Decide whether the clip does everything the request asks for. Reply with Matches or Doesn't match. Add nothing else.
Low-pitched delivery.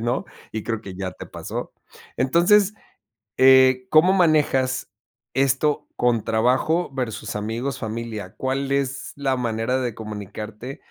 Matches